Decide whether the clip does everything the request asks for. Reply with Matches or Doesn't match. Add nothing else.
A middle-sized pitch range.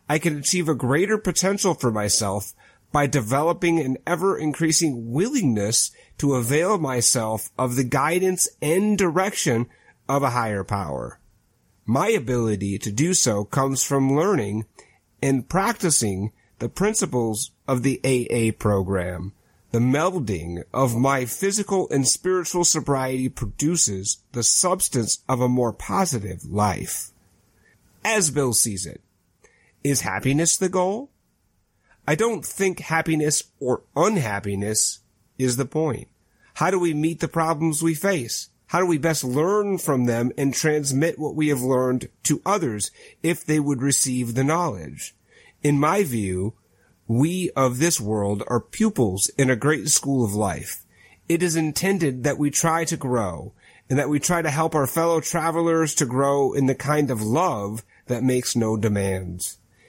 Doesn't match